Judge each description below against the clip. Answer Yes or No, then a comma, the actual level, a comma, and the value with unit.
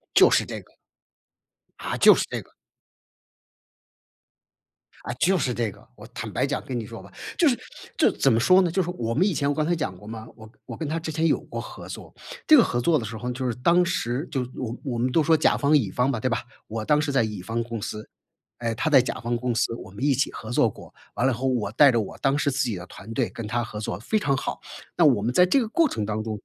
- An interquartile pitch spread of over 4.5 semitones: Yes, average, 5.2 semitones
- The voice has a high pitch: No, low, 125 Hz